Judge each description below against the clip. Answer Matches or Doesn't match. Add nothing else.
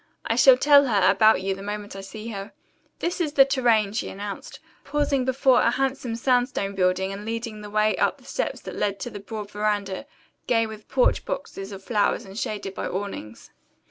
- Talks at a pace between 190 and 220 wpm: Matches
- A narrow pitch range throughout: Doesn't match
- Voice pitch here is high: Matches